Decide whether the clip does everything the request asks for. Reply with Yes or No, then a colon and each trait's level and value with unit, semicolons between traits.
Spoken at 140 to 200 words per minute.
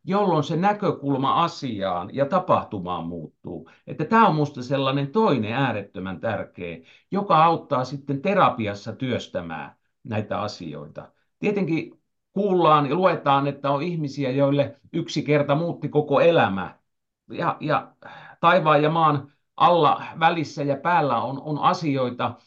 No: average, 125 wpm